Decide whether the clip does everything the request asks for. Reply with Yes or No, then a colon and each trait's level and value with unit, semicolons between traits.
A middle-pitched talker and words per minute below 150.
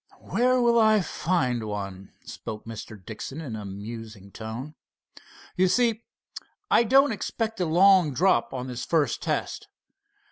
Yes: medium, 145 Hz; average, 140 wpm